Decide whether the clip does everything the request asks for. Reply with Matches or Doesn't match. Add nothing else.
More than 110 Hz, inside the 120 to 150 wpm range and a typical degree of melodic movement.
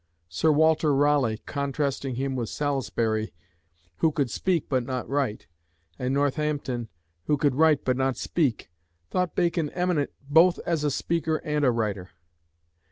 Matches